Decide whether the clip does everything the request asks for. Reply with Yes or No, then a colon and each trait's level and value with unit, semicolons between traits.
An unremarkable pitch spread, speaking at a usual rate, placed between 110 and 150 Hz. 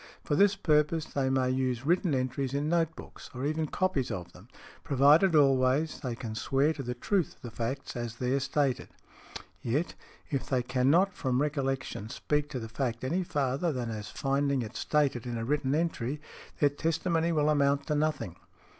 Yes: average, 3.2 semitones; average, 185 wpm; medium, 140 Hz